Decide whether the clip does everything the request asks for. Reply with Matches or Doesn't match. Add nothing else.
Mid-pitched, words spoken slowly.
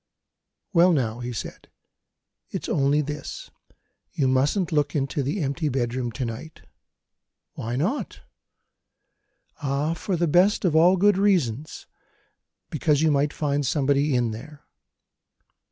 Matches